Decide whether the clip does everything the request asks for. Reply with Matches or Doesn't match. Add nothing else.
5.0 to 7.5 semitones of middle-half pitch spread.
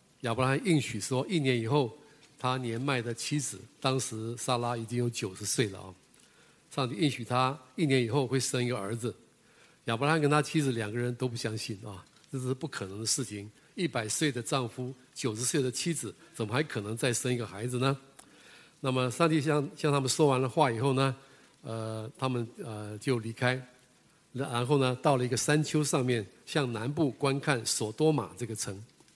Doesn't match